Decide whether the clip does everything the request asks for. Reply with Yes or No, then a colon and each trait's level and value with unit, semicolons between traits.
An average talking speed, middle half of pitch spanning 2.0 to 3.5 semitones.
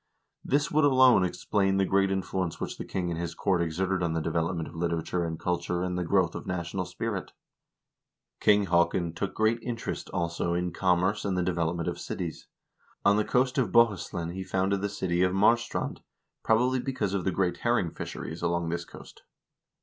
Yes: average, 190 wpm; average, 2.9 semitones